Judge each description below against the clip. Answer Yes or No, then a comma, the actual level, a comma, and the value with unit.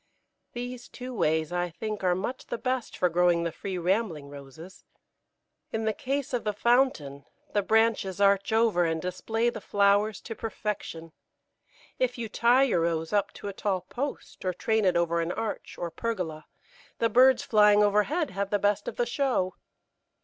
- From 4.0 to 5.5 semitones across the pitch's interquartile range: Yes, average, 4.6 semitones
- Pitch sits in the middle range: No, high, 205 Hz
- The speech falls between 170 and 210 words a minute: Yes, average, 175 wpm